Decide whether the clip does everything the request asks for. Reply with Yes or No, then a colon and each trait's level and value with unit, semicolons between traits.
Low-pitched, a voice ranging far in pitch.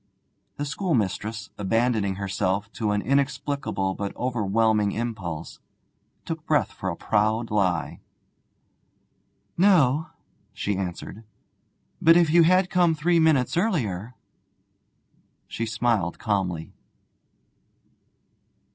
Yes: low, 115 Hz; wide, 6.5 semitones